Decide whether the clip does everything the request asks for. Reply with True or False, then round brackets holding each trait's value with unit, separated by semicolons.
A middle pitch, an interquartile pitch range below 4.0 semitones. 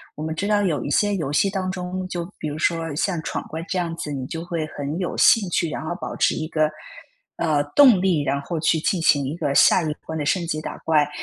True (165 Hz; 3.1 semitones)